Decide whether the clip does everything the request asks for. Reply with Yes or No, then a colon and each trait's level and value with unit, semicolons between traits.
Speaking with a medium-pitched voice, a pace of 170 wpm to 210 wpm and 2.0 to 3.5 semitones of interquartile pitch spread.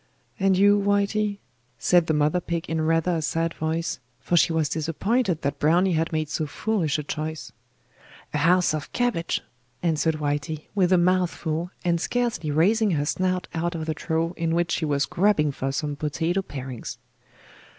Yes: medium, 165 Hz; average, 175 wpm; average, 3.0 semitones